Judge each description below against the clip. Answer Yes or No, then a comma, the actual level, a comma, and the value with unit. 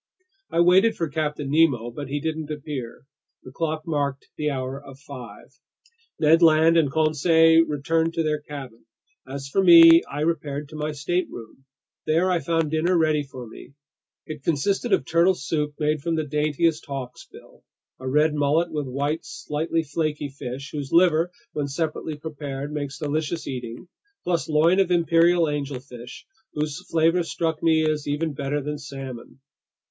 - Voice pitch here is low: No, medium, 150 Hz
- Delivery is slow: No, average, 160 wpm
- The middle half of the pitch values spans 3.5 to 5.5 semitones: No, average, 2.7 semitones